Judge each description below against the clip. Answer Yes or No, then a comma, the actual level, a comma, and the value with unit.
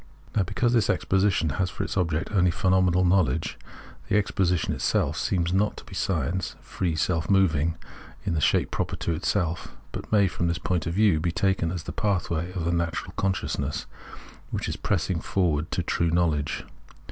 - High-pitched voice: No, very low, 90 Hz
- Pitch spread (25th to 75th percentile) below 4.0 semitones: Yes, narrow, 2.6 semitones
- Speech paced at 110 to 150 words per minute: No, average, 180 wpm